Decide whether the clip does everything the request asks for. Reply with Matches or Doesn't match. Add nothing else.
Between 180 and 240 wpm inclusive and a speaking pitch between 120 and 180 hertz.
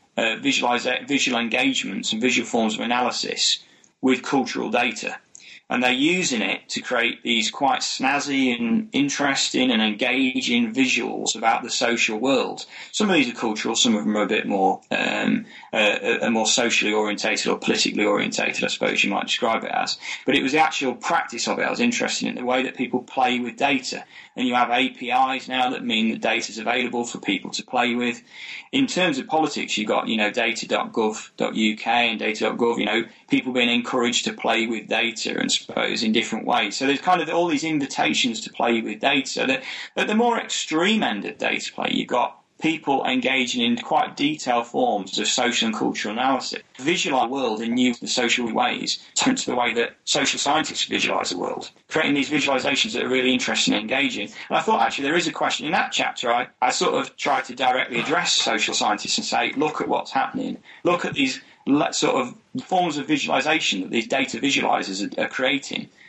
Matches